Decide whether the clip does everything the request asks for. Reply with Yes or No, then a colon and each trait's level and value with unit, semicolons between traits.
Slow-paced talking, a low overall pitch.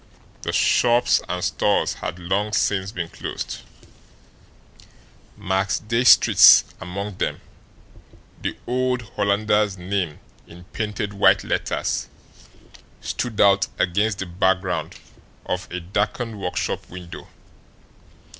Yes: slow, 100 wpm; low, 100 Hz